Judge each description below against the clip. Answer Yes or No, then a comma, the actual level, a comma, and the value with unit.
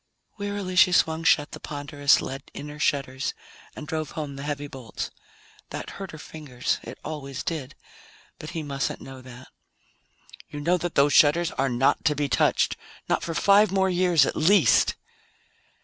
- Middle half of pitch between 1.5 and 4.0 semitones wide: Yes, average, 3.6 semitones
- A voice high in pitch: No, medium, 150 Hz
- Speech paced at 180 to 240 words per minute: No, average, 165 wpm